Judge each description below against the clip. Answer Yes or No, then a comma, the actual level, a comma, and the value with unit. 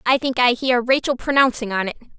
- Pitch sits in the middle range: No, high, 245 Hz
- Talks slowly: No, fast, 220 wpm